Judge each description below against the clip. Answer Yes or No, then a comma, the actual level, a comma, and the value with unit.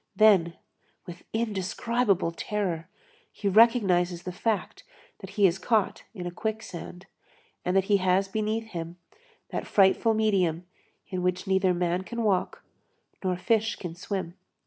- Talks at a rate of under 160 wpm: Yes, average, 140 wpm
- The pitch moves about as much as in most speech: Yes, average, 3.3 semitones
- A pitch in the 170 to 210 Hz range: Yes, high, 190 Hz